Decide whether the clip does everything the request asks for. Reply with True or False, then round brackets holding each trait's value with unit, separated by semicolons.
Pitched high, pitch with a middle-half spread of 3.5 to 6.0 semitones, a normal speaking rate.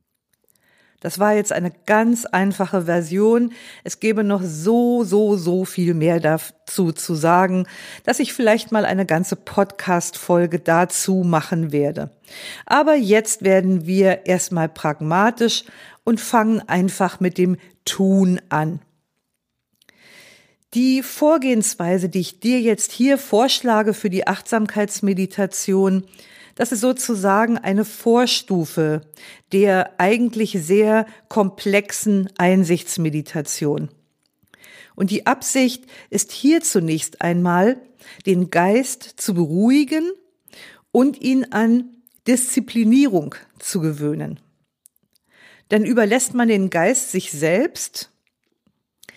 False (200 Hz; 4.3 semitones; 105 wpm)